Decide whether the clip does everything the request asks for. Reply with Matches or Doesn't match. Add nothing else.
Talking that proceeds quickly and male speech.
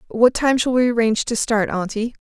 Doesn't match